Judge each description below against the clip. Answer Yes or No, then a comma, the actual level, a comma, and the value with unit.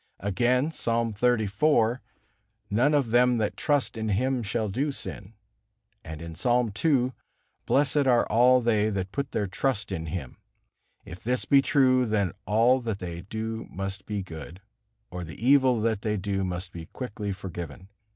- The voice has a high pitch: No, low, 110 Hz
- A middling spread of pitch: Yes, average, 4.5 semitones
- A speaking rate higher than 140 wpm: Yes, average, 160 wpm